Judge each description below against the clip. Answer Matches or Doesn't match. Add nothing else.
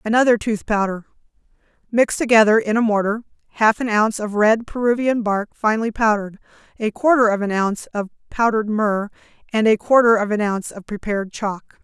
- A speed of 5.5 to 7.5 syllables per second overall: Matches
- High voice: Matches